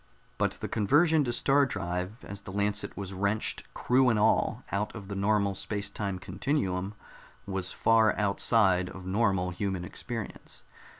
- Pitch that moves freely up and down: No, average, 2.7 semitones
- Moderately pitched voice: No, low, 100 Hz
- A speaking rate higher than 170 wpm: No, average, 155 wpm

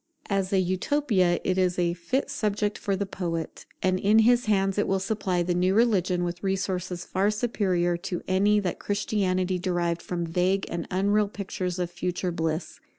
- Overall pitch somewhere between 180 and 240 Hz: Yes, medium, 185 Hz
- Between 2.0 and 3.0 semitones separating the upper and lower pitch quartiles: Yes, narrow, 2.4 semitones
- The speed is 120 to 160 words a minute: No, average, 175 wpm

